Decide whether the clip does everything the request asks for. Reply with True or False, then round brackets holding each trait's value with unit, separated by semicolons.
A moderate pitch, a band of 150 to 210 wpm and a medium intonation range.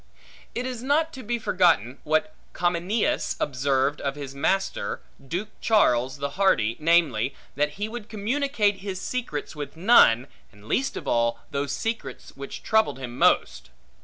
False (170 Hz; 155 wpm; 8.1 semitones)